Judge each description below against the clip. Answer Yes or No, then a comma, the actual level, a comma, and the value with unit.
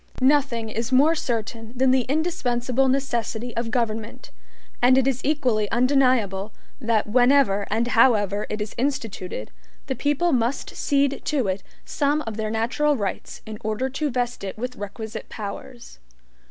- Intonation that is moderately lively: Yes, average, 3.6 semitones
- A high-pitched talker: Yes, high, 240 Hz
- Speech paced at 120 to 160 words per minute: Yes, average, 150 wpm